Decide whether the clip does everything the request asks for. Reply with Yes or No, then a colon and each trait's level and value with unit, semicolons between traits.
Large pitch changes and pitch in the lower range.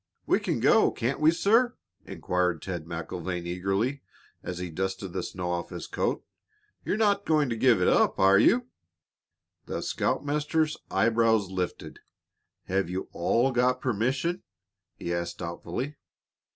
Yes: wide, 7.8 semitones; low, 100 Hz